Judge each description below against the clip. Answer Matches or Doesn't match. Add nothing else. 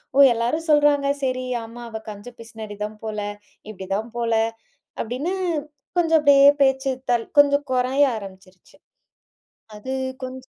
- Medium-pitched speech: Doesn't match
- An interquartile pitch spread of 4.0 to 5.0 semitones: Matches